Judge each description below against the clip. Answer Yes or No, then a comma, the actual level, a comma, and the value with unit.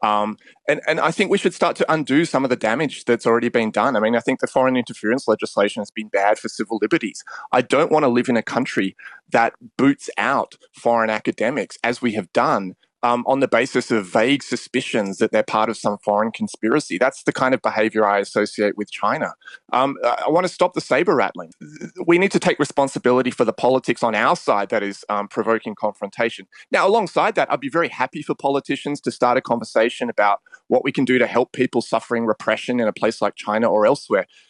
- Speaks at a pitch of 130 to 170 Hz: No, low, 120 Hz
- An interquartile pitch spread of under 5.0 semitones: No, average, 5.3 semitones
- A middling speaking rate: No, fast, 220 wpm